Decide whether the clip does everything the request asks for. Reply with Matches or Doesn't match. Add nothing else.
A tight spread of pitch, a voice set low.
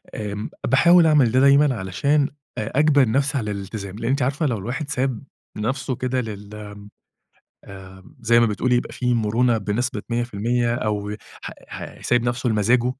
Doesn't match